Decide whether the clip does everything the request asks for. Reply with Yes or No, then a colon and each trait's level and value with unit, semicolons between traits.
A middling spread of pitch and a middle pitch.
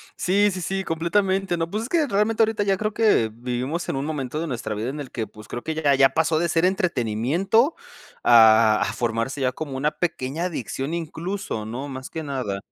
No: wide, 7.0 semitones; medium, 155 Hz